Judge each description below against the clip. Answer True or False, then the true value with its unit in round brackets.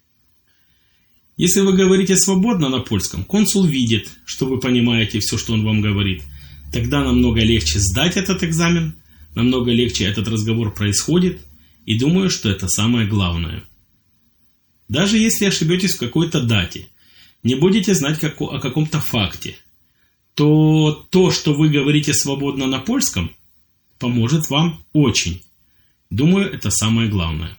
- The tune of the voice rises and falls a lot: True (8.1 semitones)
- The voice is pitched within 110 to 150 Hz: True (120 Hz)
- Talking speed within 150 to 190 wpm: False (135 wpm)